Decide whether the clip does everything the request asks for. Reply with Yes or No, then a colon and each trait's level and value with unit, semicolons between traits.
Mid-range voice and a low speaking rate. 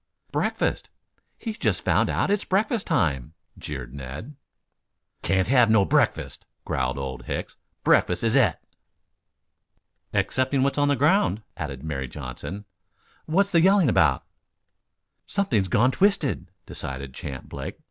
No: low, 110 Hz; slow, 125 wpm